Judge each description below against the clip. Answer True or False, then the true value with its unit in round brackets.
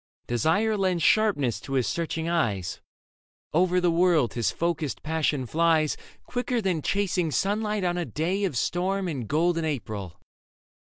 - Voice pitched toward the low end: False (170 Hz)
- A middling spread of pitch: True (4.1 semitones)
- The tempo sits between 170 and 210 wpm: False (145 wpm)